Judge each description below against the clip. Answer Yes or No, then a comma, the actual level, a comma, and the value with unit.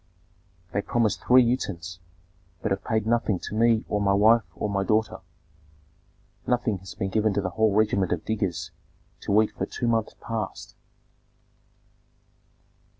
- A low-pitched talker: Yes, low, 105 Hz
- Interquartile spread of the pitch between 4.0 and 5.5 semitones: No, narrow, 2.4 semitones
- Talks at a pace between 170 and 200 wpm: No, average, 150 wpm